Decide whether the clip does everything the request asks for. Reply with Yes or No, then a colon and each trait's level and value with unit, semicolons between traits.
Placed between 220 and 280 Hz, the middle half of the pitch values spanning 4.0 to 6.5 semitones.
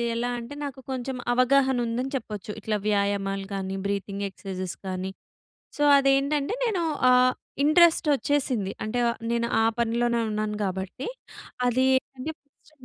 Yes: high, 235 Hz; average, 5.1 semitones